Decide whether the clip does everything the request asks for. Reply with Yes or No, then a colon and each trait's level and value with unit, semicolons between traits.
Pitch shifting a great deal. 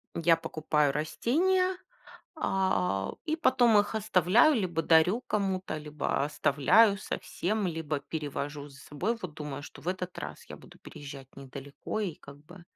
Yes: wide, 6.0 semitones